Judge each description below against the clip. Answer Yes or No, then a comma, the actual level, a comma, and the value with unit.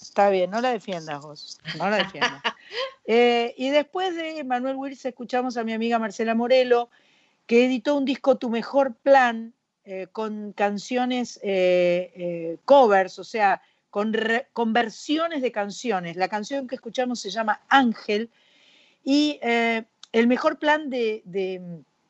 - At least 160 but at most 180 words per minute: No, average, 150 wpm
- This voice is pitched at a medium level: No, high, 235 Hz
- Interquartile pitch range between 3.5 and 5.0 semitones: Yes, average, 4.6 semitones